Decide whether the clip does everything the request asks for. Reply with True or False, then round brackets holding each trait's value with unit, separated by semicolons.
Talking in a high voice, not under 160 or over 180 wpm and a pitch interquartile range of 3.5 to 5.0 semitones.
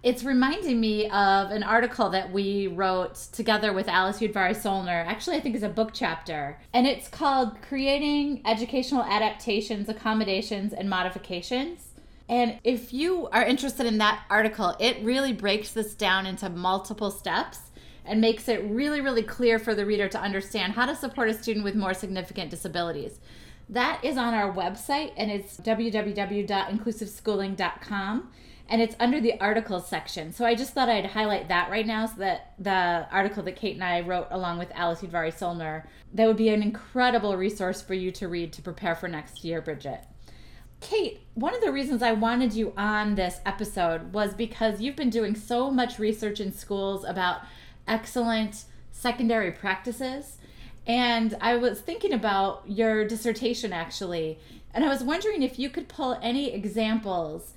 True (215 Hz; 170 wpm; 3.8 semitones)